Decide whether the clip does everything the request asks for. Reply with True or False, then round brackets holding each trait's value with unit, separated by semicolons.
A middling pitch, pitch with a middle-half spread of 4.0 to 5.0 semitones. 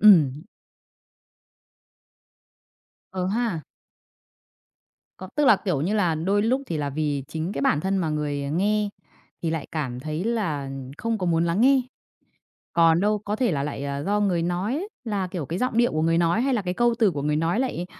False (180 Hz; 5.4 semitones)